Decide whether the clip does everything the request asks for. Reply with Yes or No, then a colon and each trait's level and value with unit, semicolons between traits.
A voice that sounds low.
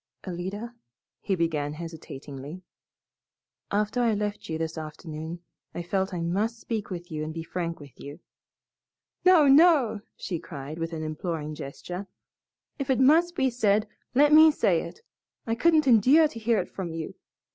No: high, 190 Hz